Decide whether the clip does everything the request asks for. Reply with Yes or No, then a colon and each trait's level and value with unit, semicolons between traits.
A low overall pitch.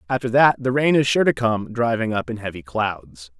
Yes: low, 115 Hz